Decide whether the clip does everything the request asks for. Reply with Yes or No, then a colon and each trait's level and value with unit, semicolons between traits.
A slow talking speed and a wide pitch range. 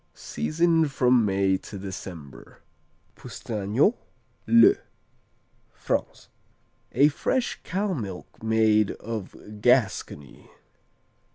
Yes: slow, 80 wpm; wide, 7.7 semitones